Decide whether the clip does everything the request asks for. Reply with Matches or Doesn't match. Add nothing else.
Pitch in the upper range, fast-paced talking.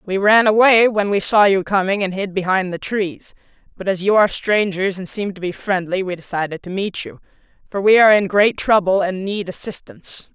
Matches